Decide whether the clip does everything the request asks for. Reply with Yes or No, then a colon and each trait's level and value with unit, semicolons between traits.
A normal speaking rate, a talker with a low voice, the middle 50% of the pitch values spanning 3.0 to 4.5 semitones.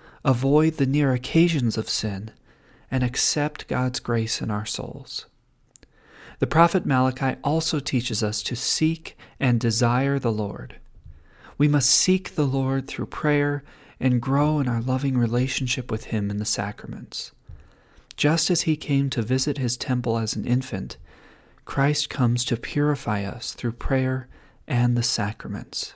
Yes: average, 150 wpm; low, 130 Hz; average, 3.5 semitones